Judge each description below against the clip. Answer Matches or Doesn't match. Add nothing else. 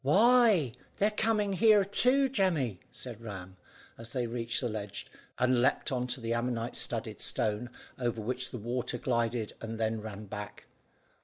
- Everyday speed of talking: Matches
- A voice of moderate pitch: Doesn't match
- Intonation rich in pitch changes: Matches